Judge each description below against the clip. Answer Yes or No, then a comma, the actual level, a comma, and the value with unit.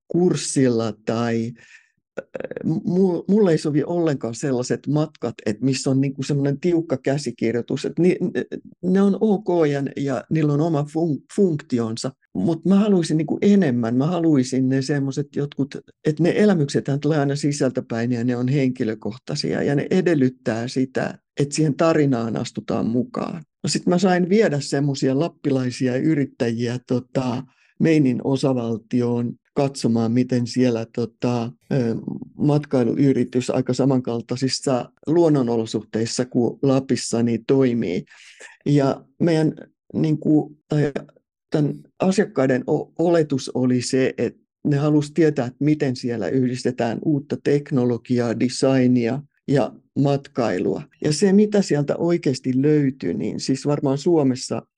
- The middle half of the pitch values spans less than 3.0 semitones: No, average, 3.8 semitones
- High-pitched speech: No, low, 135 Hz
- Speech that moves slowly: No, average, 115 wpm